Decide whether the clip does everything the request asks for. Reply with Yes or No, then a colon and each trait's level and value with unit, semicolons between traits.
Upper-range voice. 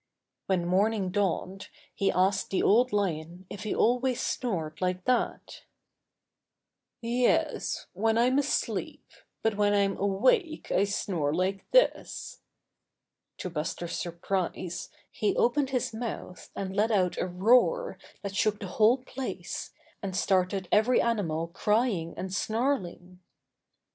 Yes: high, 200 Hz